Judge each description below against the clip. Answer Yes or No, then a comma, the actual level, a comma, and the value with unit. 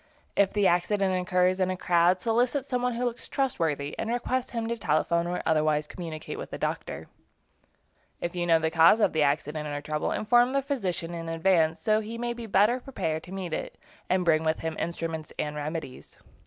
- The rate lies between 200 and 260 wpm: Yes, fast, 205 wpm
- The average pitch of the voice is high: No, medium, 180 Hz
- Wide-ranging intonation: Yes, wide, 6.0 semitones